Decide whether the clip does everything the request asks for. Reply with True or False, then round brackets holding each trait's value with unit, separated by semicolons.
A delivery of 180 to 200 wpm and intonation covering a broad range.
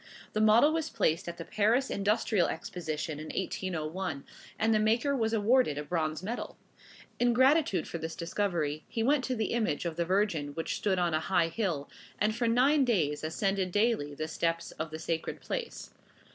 True (185 wpm; 6.1 semitones)